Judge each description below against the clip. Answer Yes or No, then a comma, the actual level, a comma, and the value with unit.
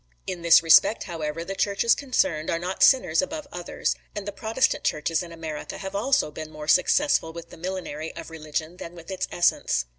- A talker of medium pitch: Yes, medium, 170 Hz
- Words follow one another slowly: No, average, 190 wpm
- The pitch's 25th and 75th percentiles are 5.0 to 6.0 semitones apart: No, average, 3.8 semitones